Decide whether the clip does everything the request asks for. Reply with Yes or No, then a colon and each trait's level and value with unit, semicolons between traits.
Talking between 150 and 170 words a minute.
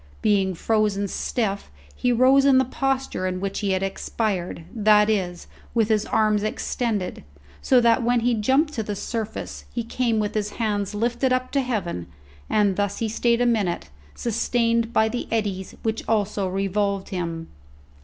Yes: average, 165 wpm